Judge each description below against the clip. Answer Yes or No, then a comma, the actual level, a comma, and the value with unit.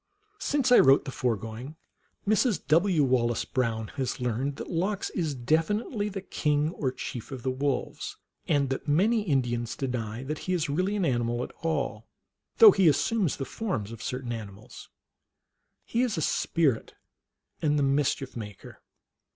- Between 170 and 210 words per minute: No, average, 160 wpm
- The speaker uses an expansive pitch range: Yes, wide, 6.2 semitones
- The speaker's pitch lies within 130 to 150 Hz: Yes, medium, 140 Hz